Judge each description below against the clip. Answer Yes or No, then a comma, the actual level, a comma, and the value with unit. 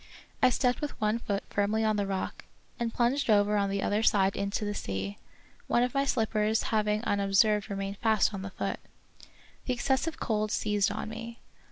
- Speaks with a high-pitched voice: Yes, high, 210 Hz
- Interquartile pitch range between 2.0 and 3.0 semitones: Yes, narrow, 2.5 semitones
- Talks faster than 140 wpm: Yes, average, 185 wpm